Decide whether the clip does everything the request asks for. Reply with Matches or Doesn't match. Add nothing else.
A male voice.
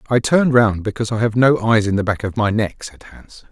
Matches